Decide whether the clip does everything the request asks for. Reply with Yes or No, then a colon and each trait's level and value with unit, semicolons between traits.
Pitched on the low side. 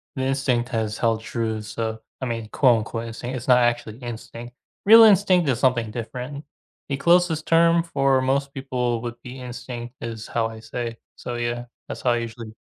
Yes: low, 120 Hz